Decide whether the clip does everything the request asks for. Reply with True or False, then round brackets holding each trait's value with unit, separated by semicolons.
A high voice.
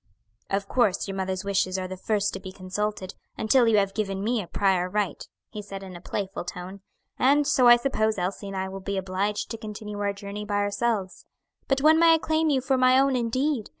True (205 Hz)